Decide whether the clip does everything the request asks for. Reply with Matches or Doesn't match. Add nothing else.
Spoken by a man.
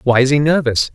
Matches